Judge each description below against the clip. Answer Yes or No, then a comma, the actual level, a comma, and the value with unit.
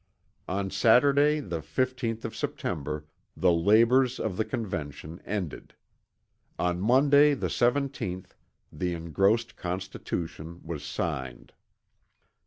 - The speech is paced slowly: Yes, slow, 100 wpm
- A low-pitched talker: Yes, very low, 95 Hz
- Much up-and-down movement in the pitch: Yes, wide, 6.6 semitones